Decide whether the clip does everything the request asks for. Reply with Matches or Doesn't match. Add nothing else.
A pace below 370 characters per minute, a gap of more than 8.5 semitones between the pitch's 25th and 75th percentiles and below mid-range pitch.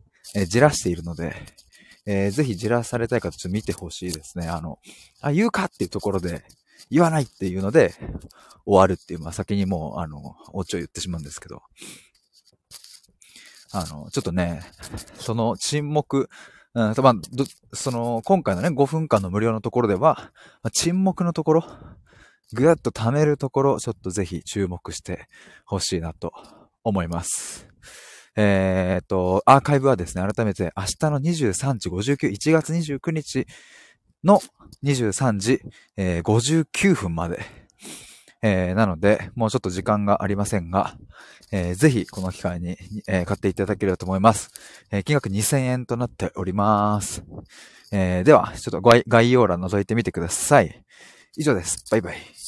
Doesn't match